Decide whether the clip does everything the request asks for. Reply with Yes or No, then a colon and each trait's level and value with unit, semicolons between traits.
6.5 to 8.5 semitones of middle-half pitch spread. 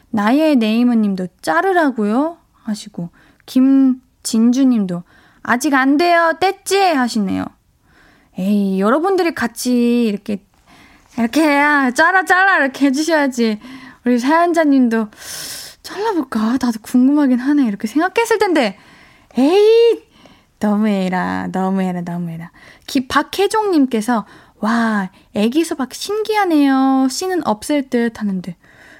Yes: wide, 6.8 semitones